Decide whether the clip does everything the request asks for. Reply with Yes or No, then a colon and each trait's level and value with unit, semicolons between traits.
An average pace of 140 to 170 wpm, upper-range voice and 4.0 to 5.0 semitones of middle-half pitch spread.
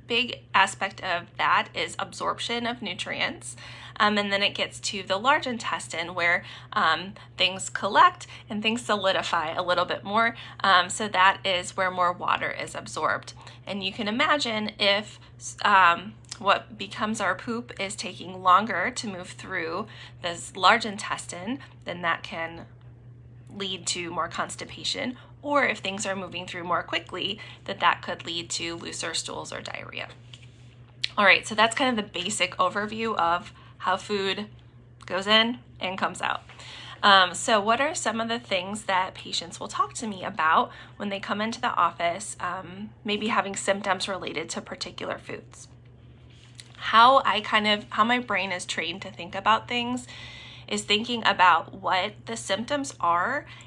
Yes: average, 165 wpm; high, 195 Hz; average, 4.3 semitones